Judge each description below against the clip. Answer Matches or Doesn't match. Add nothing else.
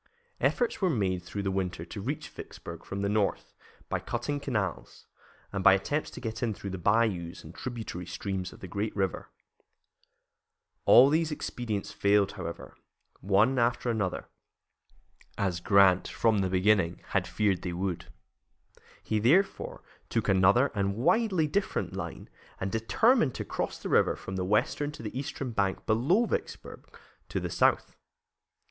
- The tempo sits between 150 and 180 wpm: Matches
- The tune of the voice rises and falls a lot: Doesn't match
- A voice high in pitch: Doesn't match